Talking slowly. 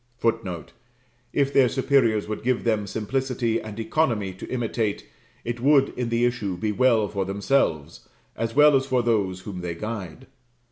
No: average, 160 wpm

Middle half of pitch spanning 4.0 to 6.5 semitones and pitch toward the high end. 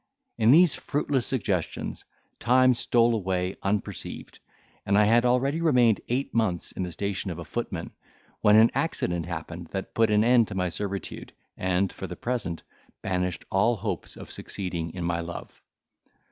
No: average, 4.8 semitones; low, 100 Hz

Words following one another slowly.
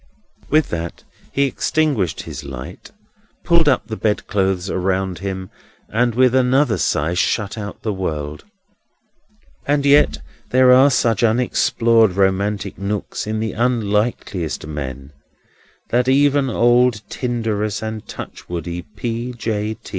Yes: slow, 120 wpm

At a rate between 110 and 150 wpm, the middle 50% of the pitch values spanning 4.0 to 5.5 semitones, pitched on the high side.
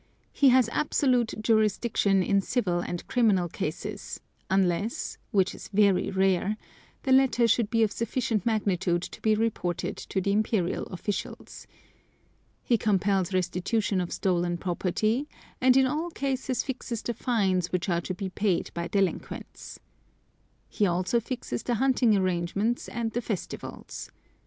Yes: average, 140 wpm; average, 4.3 semitones; high, 205 Hz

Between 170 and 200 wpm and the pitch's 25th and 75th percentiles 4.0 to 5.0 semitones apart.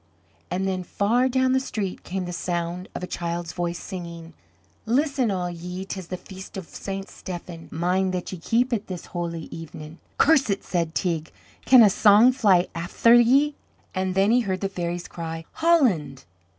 Yes: average, 175 wpm; average, 4.3 semitones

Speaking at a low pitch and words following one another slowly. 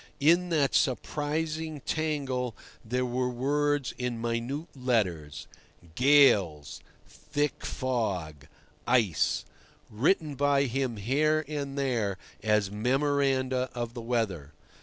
Yes: low, 130 Hz; slow, 95 wpm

